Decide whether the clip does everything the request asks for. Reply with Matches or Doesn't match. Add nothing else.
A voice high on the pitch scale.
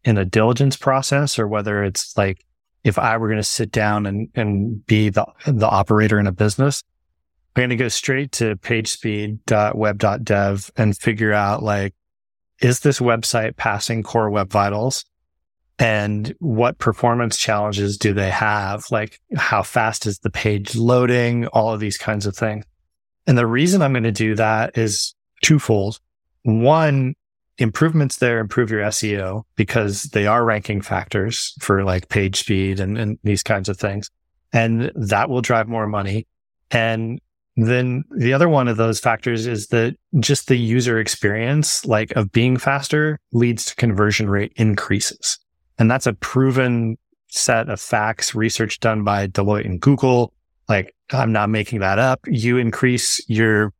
Doesn't match